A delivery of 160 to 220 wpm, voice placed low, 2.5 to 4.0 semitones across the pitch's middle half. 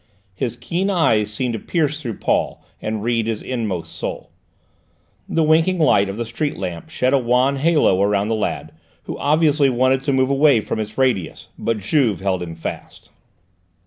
No: average, 175 wpm; low, 120 Hz; average, 5.2 semitones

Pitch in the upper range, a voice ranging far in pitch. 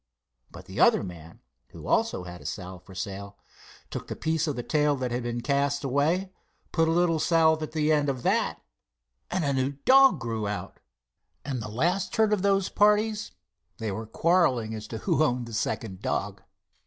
No: medium, 140 Hz; wide, 7.0 semitones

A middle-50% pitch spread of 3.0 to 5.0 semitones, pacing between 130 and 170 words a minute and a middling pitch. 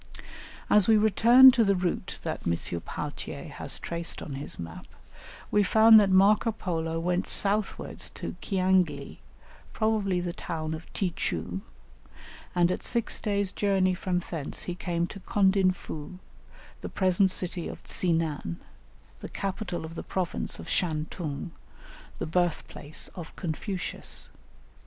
Yes: average, 3.3 semitones; average, 140 wpm; medium, 180 Hz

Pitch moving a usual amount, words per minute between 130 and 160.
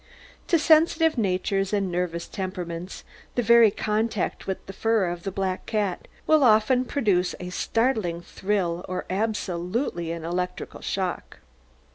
Yes: average, 4.0 semitones; slow, 135 wpm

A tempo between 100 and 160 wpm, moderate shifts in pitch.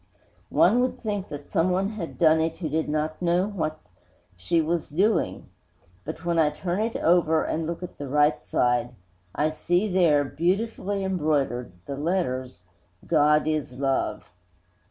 Yes: average, 155 wpm; average, 3.7 semitones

